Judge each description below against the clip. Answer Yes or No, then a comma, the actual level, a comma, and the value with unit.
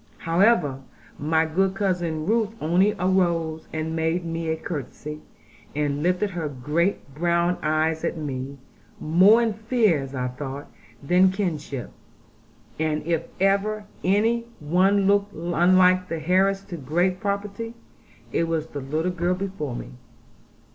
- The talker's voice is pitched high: No, medium, 170 Hz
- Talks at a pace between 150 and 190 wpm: No, slow, 135 wpm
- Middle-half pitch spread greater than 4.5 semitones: No, average, 3.9 semitones